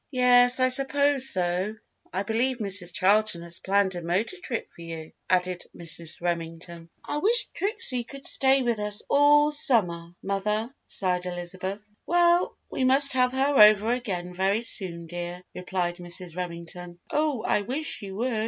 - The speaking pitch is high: Yes, high, 200 Hz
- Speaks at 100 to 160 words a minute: Yes, average, 155 wpm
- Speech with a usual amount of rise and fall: No, wide, 6.4 semitones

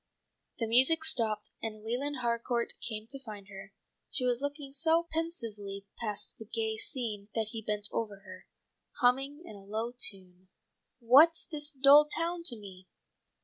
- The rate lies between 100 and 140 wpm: No, average, 155 wpm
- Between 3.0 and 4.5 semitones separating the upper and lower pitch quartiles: No, average, 5.1 semitones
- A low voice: No, high, 235 Hz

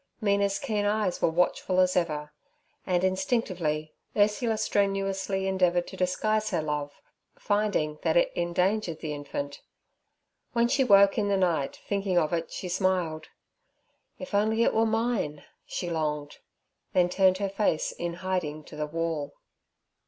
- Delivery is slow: No, average, 145 wpm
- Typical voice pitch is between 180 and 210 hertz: Yes, medium, 185 Hz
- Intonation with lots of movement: No, average, 4.0 semitones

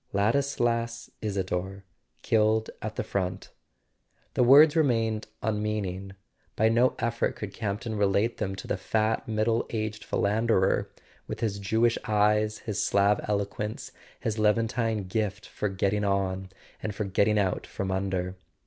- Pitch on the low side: Yes, low, 105 Hz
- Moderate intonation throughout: No, narrow, 2.3 semitones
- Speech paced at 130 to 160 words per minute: Yes, average, 140 wpm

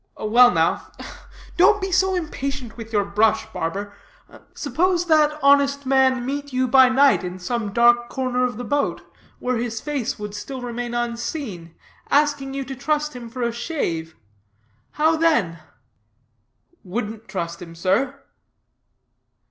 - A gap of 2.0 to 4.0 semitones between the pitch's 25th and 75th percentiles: No, average, 4.6 semitones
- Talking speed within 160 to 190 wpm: No, average, 140 wpm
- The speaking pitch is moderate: No, very high, 250 Hz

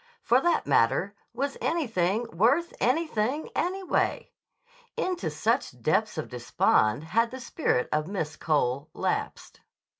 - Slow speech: Yes, slow, 120 wpm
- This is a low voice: No, high, 220 Hz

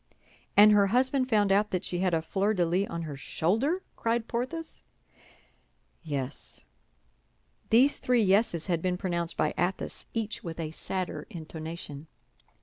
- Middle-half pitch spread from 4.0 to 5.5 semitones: Yes, average, 5.2 semitones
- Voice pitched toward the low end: No, medium, 185 Hz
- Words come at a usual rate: Yes, average, 145 wpm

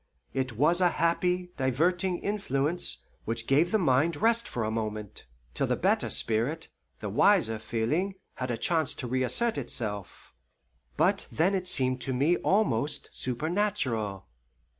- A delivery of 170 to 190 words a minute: No, average, 140 wpm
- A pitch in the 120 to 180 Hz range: Yes, medium, 140 Hz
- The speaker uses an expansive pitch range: Yes, wide, 7.3 semitones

